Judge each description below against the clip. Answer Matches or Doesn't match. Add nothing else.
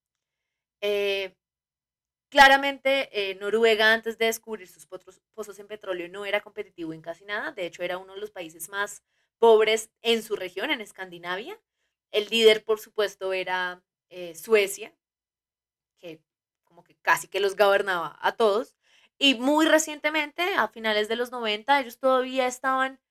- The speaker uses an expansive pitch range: Doesn't match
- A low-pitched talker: Doesn't match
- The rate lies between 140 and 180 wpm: Matches